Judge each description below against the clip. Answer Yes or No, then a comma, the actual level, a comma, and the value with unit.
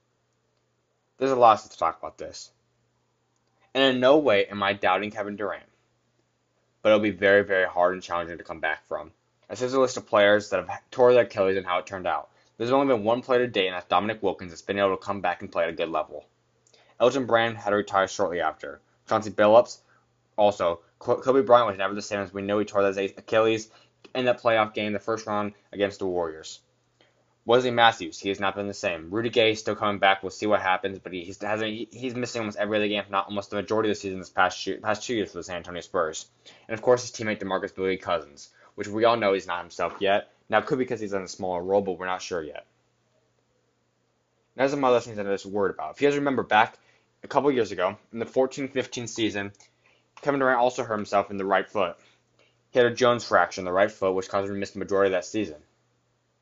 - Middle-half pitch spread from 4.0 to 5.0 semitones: No, average, 3.4 semitones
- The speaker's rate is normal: No, fast, 240 wpm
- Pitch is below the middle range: Yes, low, 105 Hz